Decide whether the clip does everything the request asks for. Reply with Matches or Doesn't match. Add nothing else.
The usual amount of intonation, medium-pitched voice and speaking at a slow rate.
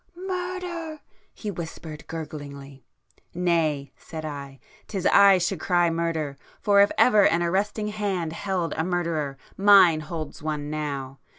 Matches